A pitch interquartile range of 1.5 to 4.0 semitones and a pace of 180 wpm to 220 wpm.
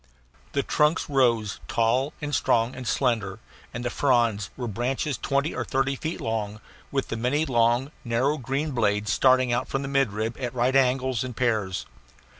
No: average, 3.0 semitones; average, 165 wpm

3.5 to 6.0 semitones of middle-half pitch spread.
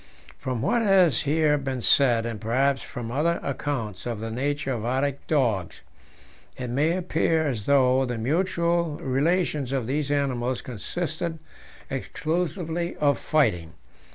Yes: average, 4.7 semitones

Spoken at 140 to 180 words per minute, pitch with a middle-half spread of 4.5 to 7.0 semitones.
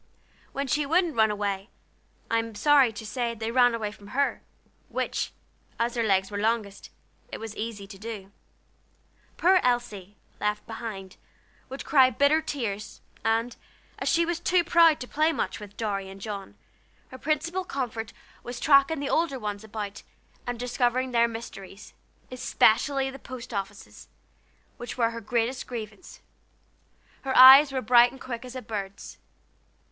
No: average, 155 wpm; average, 4.1 semitones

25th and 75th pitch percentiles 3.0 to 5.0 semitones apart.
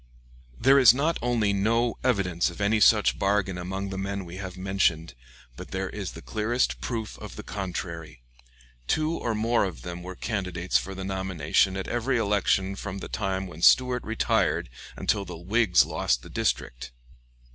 Yes: average, 3.6 semitones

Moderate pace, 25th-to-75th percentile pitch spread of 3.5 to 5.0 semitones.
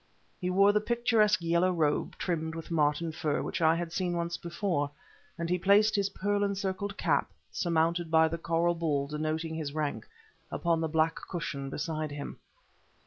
No: average, 170 wpm; average, 2.8 semitones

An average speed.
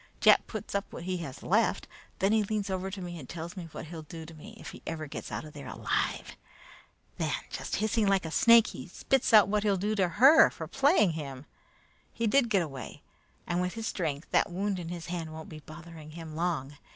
No: fast, 225 wpm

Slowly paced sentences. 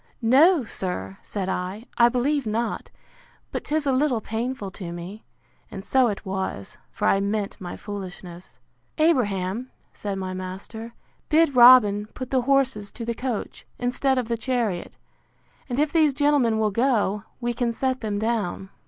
No: average, 160 wpm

